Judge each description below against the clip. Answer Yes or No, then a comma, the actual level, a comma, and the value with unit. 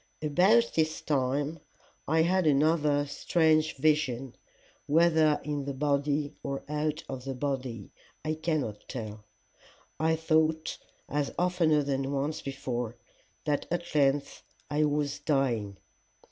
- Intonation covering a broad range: No, narrow, 2.5 semitones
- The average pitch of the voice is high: No, medium, 145 Hz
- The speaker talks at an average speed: No, slow, 120 wpm